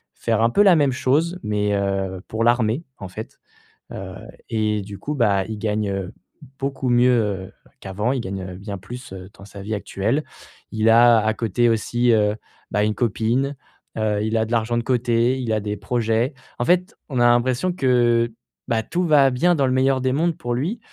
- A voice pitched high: No, low, 115 Hz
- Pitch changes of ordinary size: Yes, average, 3.6 semitones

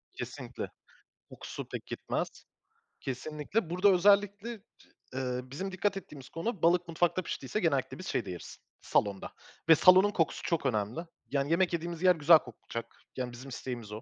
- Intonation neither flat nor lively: No, wide, 6.1 semitones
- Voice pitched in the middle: Yes, medium, 165 Hz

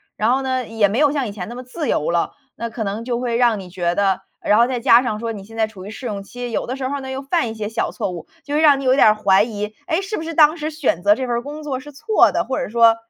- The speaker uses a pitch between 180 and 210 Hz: No, high, 235 Hz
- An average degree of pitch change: Yes, average, 4.3 semitones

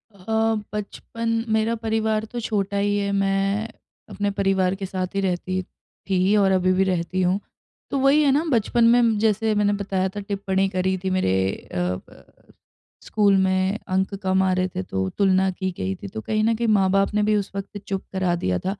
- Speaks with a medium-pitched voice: No, high, 195 Hz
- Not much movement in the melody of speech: Yes, narrow, 2.2 semitones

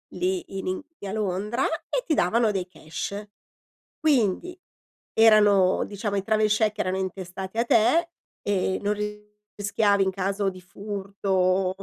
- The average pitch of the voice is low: No, high, 200 Hz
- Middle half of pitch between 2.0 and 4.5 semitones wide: Yes, narrow, 2.5 semitones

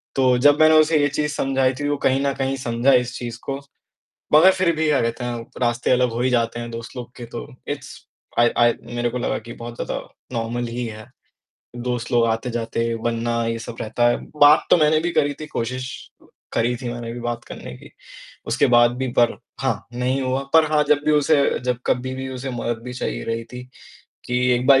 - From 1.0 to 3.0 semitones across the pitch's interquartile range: Yes, narrow, 2.5 semitones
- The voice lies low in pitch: Yes, low, 125 Hz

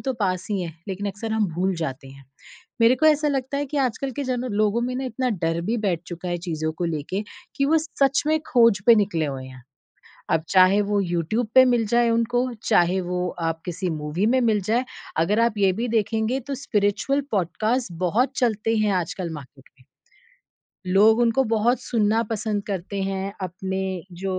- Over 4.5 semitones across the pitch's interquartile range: Yes, average, 5.0 semitones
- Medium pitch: No, high, 205 Hz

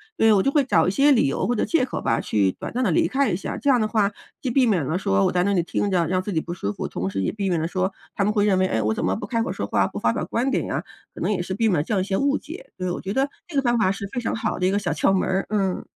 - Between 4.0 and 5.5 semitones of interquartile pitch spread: Yes, average, 4.9 semitones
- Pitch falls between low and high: No, high, 200 Hz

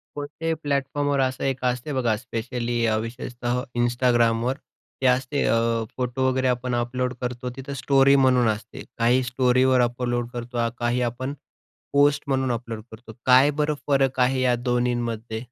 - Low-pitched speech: Yes, low, 125 Hz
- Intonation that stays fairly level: Yes, narrow, 1.7 semitones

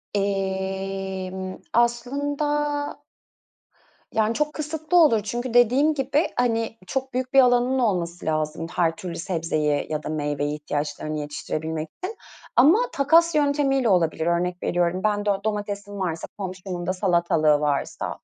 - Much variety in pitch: Yes, wide, 7.3 semitones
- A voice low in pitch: No, high, 200 Hz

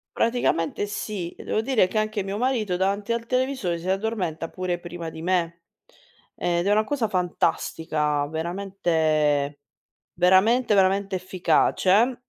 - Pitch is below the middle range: No, medium, 185 Hz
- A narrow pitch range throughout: No, average, 4.1 semitones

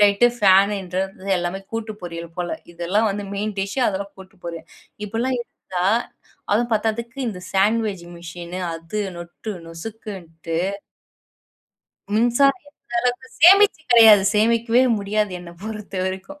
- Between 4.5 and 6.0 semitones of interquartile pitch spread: No, average, 3.8 semitones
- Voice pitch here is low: No, high, 205 Hz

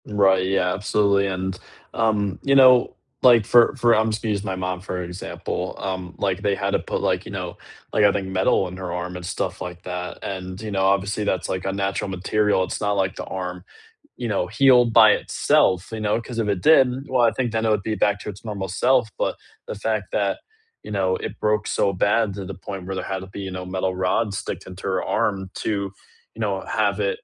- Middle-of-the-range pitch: No, low, 100 Hz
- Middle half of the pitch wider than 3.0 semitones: No, average, 2.7 semitones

